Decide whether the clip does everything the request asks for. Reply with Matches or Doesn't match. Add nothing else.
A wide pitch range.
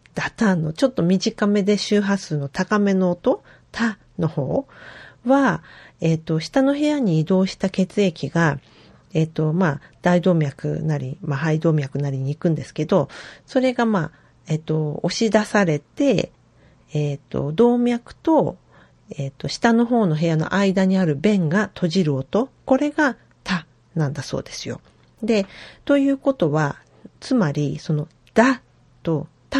Matches